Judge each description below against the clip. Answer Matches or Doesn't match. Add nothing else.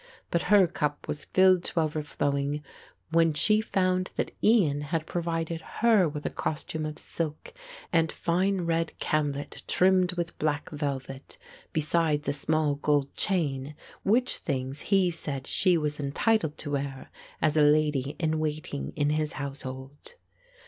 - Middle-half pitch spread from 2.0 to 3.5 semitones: Matches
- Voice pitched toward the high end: Doesn't match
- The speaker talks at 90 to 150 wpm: Matches